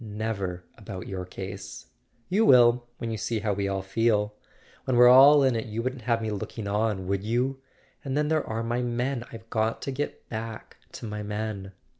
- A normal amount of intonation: Yes, average, 3.0 semitones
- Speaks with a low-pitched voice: Yes, low, 115 Hz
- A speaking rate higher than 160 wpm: Yes, average, 190 wpm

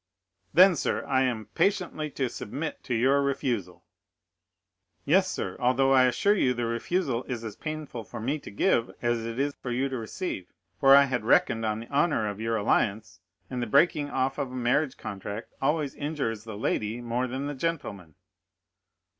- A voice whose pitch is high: No, low, 125 Hz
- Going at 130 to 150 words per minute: No, average, 180 wpm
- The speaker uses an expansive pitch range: No, average, 4.0 semitones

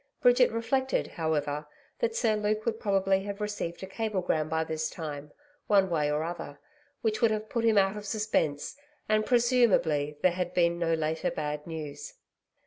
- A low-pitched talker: No, high, 190 Hz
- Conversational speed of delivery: Yes, average, 170 wpm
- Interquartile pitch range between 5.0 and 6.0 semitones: Yes, wide, 5.4 semitones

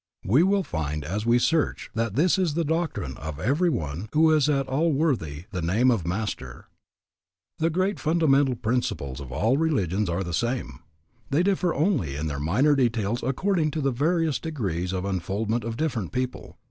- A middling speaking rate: Yes, average, 180 wpm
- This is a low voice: Yes, low, 120 Hz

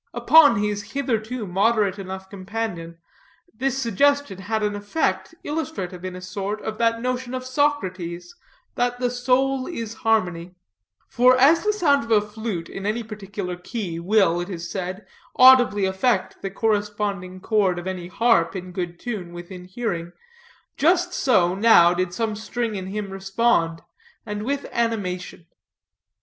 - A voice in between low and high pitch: No, high, 210 Hz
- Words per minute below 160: Yes, average, 150 wpm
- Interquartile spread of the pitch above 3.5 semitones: Yes, average, 4.7 semitones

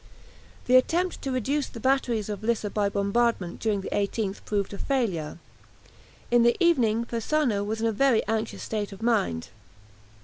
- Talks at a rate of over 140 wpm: Yes, average, 165 wpm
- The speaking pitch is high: Yes, high, 225 Hz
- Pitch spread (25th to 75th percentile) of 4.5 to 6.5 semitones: No, average, 3.7 semitones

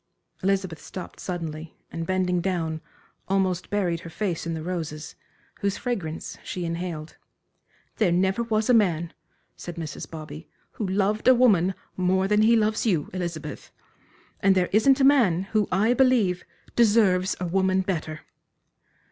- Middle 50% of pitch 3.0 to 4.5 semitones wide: Yes, average, 3.8 semitones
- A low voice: No, medium, 185 Hz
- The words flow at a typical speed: Yes, average, 150 wpm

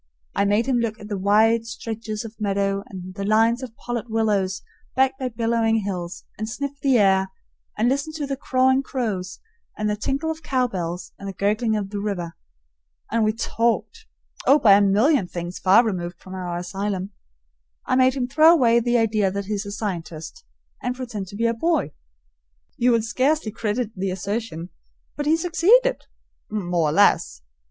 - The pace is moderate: Yes, average, 180 wpm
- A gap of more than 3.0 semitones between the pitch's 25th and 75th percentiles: Yes, average, 4.1 semitones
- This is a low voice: No, high, 220 Hz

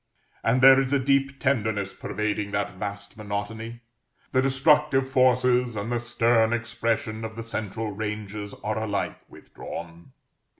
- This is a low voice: Yes, low, 115 Hz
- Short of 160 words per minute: Yes, slow, 135 wpm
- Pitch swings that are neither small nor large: Yes, average, 3.4 semitones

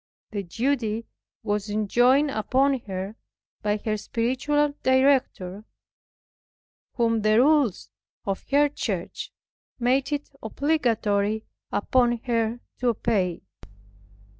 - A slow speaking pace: Yes, slow, 95 wpm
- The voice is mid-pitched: No, high, 230 Hz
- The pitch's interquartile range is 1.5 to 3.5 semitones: No, average, 4.1 semitones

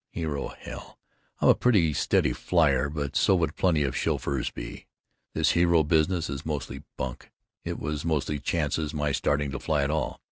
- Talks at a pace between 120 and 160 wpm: No, average, 175 wpm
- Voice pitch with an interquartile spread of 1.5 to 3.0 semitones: Yes, narrow, 2.5 semitones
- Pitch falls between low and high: No, very low, 75 Hz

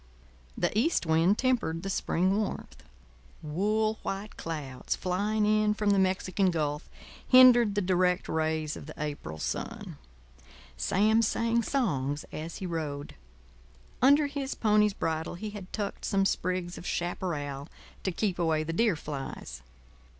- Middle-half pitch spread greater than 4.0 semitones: Yes, average, 5.0 semitones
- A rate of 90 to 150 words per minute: Yes, average, 140 wpm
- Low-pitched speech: No, medium, 185 Hz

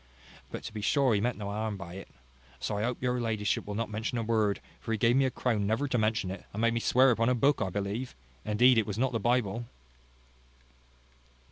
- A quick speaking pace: Yes, fast, 240 wpm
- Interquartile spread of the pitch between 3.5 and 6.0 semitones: No, average, 3.0 semitones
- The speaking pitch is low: Yes, low, 115 Hz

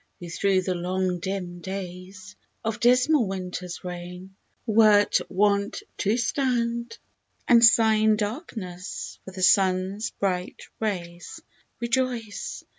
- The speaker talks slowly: Yes, slow, 115 wpm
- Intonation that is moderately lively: Yes, average, 3.7 semitones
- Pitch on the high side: Yes, high, 200 Hz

